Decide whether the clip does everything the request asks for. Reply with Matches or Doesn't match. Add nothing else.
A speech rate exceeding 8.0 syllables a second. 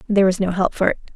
Matches